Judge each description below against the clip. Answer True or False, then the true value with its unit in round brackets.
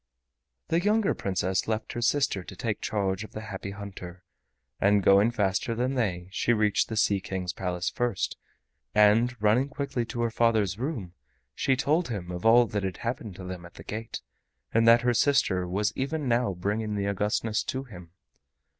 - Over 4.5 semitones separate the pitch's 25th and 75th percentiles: False (3.8 semitones)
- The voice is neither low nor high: False (105 Hz)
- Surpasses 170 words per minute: True (180 wpm)